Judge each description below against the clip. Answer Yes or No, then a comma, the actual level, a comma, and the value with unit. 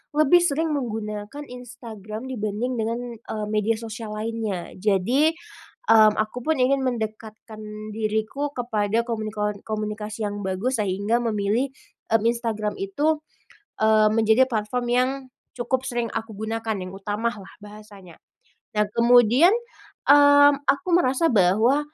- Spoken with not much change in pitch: No, average, 3.0 semitones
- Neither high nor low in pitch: No, high, 225 Hz